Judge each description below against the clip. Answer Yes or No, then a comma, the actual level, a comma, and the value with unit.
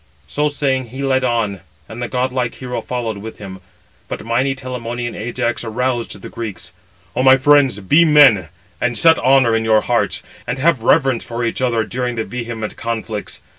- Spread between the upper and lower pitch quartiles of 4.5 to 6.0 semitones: No, average, 2.7 semitones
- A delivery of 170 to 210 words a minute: Yes, average, 180 wpm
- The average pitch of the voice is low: Yes, low, 120 Hz